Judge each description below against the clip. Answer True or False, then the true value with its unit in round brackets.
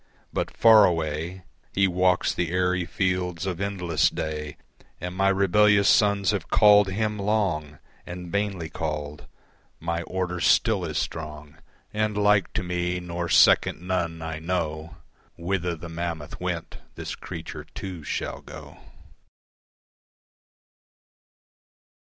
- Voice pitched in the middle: False (90 Hz)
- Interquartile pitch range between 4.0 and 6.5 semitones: False (2.9 semitones)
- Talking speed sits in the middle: False (120 wpm)